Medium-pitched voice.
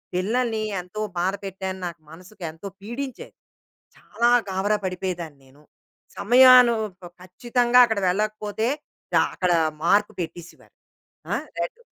No: high, 200 Hz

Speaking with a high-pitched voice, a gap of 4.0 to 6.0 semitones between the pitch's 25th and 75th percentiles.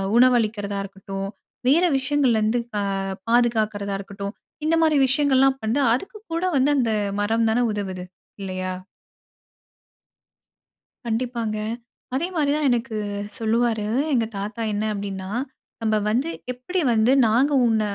Yes: high, 230 Hz; average, 4.3 semitones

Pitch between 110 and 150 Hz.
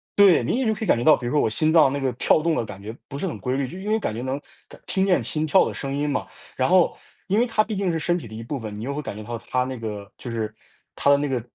Yes: medium, 140 Hz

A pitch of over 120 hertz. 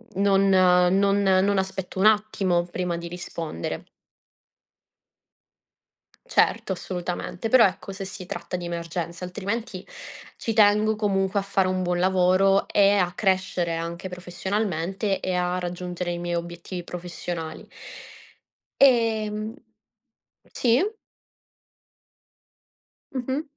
Yes: medium, 185 Hz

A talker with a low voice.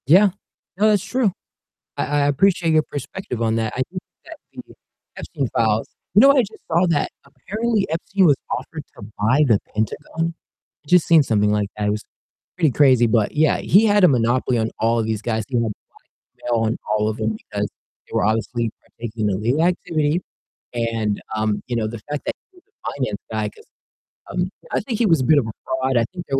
Yes: low, 130 Hz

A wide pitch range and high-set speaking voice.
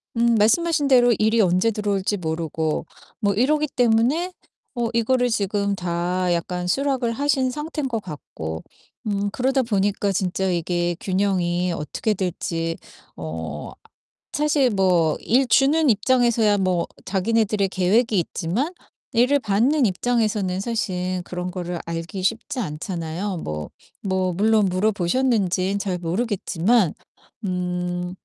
No: average, 4.9 semitones; high, 200 Hz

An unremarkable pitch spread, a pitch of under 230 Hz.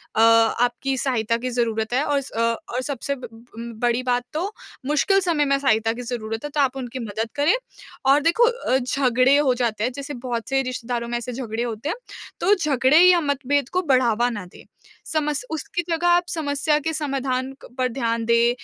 No: average, 3.5 semitones; very high, 255 Hz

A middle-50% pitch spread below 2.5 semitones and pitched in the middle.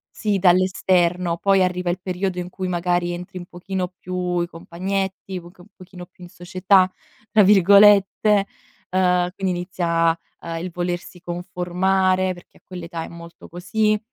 Yes: narrow, 1.4 semitones; medium, 180 Hz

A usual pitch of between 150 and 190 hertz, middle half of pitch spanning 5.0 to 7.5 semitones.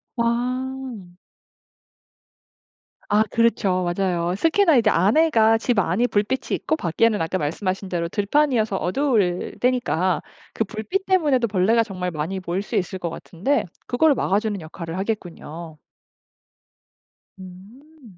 No: high, 210 Hz; average, 5.3 semitones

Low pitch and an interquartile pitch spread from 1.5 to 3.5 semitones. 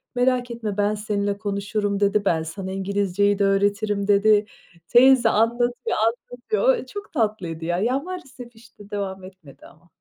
No: high, 205 Hz; average, 3.2 semitones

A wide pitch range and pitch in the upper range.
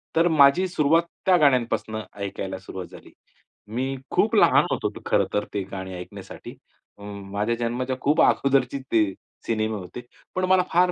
No: wide, 6.8 semitones; low, 125 Hz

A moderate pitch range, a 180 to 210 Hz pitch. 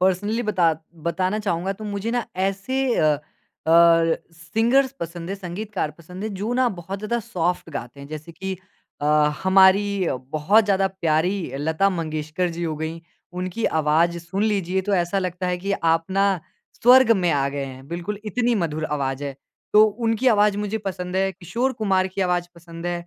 Yes: average, 3.6 semitones; medium, 185 Hz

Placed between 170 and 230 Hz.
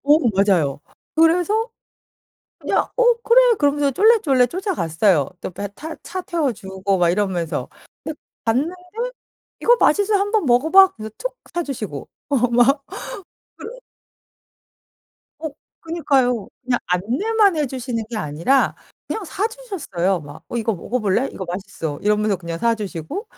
No: very high, 250 Hz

